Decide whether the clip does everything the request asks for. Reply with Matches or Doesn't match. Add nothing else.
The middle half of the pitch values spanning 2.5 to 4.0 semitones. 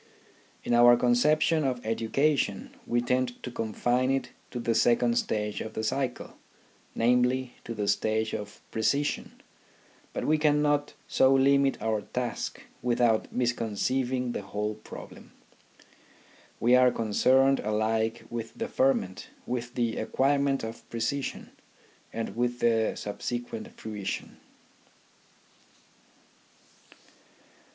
Matches